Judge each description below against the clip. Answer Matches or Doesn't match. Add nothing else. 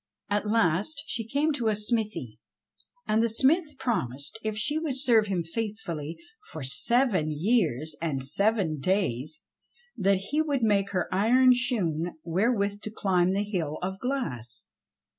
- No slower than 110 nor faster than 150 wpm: Matches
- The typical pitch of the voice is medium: Doesn't match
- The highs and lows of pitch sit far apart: Matches